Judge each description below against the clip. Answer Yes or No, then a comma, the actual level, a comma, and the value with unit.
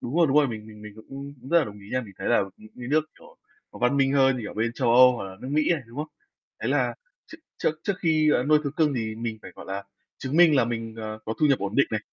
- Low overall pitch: Yes, low, 125 Hz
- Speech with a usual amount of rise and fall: Yes, average, 5.0 semitones